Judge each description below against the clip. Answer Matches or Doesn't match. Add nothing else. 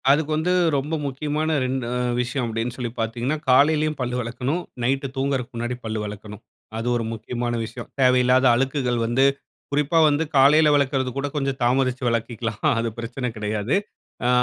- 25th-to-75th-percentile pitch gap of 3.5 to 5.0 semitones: Doesn't match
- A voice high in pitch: Doesn't match